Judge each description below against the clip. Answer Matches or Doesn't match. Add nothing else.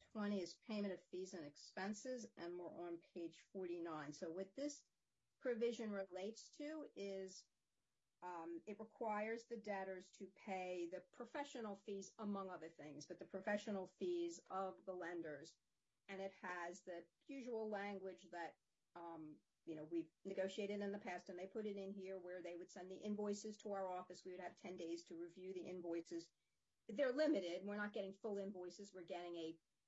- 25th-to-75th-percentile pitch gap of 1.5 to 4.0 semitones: Matches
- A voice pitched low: Doesn't match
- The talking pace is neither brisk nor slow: Matches